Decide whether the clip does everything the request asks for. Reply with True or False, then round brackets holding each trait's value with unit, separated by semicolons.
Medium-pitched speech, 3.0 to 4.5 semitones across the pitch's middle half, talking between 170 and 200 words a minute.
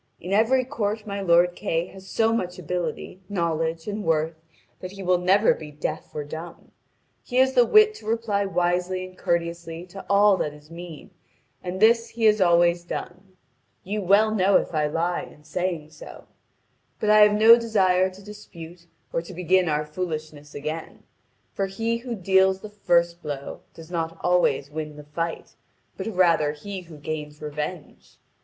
True (180 Hz; 3.7 semitones; 175 wpm)